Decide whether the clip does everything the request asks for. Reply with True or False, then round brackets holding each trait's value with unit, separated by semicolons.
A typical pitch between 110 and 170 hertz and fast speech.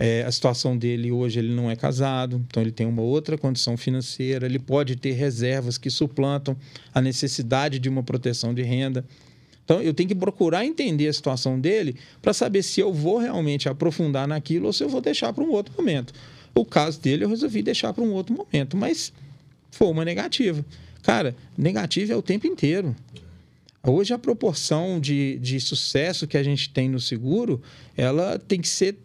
True (140 Hz; 190 wpm)